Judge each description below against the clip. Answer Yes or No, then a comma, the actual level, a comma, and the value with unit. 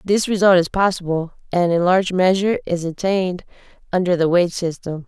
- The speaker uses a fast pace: No, average, 165 wpm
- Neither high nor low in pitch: Yes, medium, 180 Hz